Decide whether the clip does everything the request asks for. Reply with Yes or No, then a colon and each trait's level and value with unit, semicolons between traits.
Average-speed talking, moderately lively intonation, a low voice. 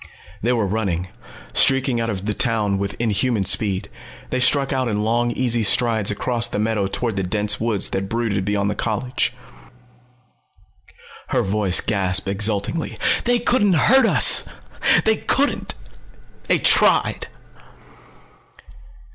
No: slow, 130 wpm; average, 3.7 semitones; low, 110 Hz